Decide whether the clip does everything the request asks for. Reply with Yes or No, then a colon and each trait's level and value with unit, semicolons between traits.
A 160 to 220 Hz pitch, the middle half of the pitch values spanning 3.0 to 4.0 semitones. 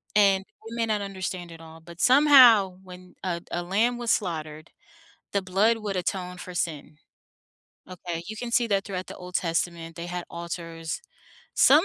Yes: medium, 185 Hz; average, 3.4 semitones